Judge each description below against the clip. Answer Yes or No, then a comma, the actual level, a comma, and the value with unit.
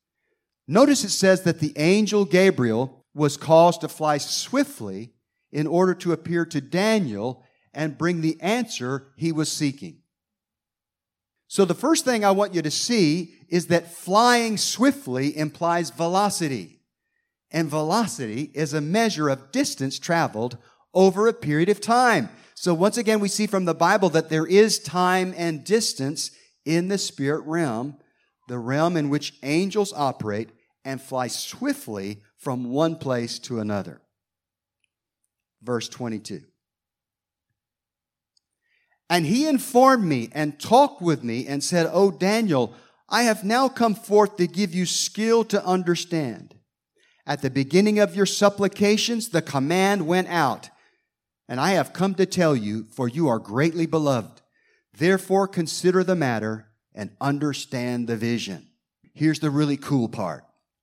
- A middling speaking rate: Yes, average, 145 wpm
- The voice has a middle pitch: Yes, medium, 165 Hz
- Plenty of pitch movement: Yes, wide, 6.3 semitones